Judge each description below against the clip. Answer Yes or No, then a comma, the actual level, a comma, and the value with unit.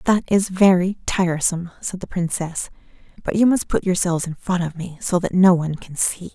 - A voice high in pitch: No, medium, 180 Hz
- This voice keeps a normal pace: No, fast, 210 wpm